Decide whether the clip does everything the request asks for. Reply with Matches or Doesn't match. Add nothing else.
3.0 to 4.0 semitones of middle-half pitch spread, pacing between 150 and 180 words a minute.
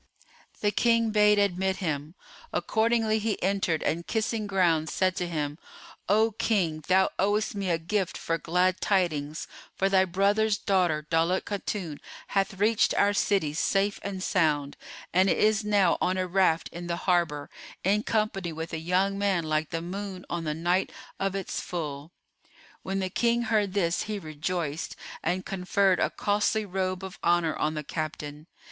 Matches